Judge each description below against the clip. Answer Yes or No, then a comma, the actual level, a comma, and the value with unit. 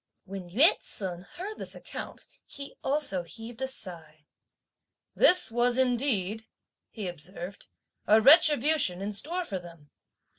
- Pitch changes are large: Yes, wide, 7.3 semitones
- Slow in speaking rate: Yes, slow, 125 wpm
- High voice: Yes, high, 220 Hz